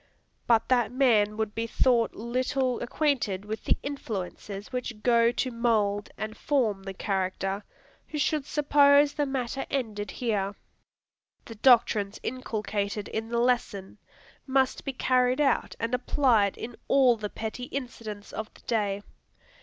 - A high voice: Yes, high, 230 Hz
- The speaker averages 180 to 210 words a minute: No, average, 140 wpm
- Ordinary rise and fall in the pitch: Yes, average, 3.7 semitones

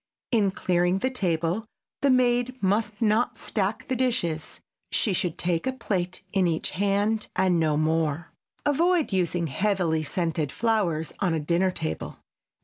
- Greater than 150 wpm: No, average, 145 wpm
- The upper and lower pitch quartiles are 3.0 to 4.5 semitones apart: No, average, 5.0 semitones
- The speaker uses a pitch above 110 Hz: Yes, high, 190 Hz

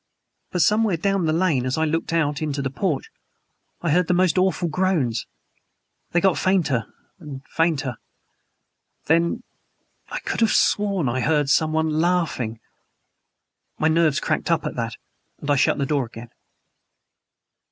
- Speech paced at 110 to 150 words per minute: Yes, average, 145 wpm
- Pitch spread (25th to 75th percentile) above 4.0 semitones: Yes, average, 4.4 semitones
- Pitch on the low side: No, medium, 160 Hz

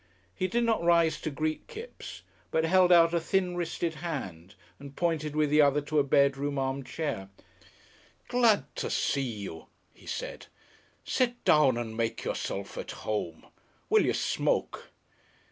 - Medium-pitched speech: Yes, medium, 155 Hz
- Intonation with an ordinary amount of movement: Yes, average, 4.4 semitones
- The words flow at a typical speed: Yes, average, 155 wpm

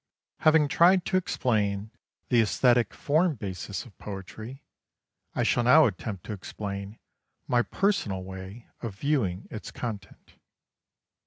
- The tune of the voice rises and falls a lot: Yes, wide, 5.9 semitones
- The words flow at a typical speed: No, slow, 125 wpm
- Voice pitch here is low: Yes, low, 110 Hz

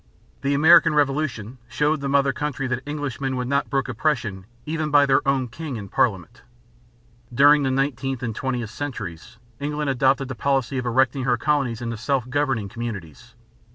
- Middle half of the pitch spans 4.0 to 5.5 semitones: No, average, 3.2 semitones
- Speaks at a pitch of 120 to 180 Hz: Yes, low, 135 Hz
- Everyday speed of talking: Yes, average, 165 wpm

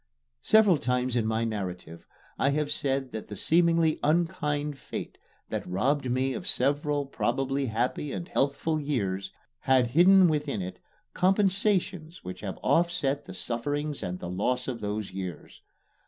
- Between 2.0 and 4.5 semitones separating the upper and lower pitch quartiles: No, wide, 5.5 semitones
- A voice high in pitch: No, low, 135 Hz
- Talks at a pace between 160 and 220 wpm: No, average, 145 wpm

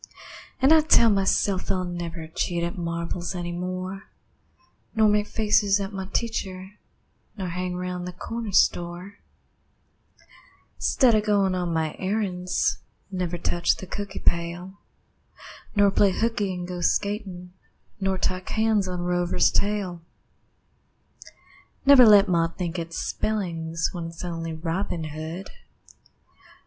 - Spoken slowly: Yes, slow, 130 wpm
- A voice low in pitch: No, medium, 185 Hz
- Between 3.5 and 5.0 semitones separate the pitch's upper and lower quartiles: No, average, 2.8 semitones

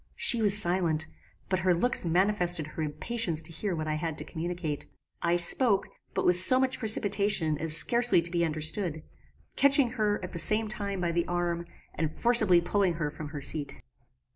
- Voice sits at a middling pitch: Yes, medium, 175 Hz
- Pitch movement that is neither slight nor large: Yes, average, 4.4 semitones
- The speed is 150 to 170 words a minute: No, average, 185 wpm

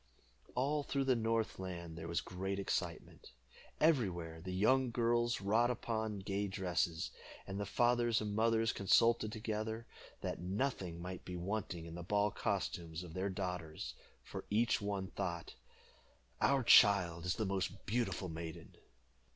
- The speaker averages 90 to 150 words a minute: Yes, average, 145 wpm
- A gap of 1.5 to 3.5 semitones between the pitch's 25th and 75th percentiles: No, average, 4.2 semitones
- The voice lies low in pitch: Yes, low, 100 Hz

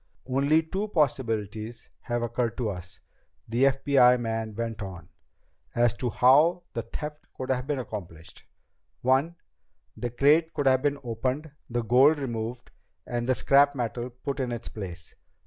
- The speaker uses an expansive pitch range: No, average, 3.4 semitones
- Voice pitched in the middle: No, low, 125 Hz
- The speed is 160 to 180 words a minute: No, average, 150 wpm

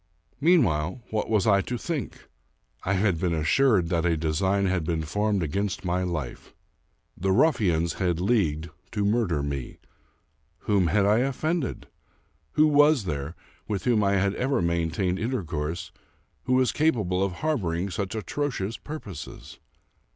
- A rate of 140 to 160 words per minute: Yes, average, 145 wpm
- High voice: No, very low, 95 Hz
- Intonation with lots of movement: Yes, wide, 5.8 semitones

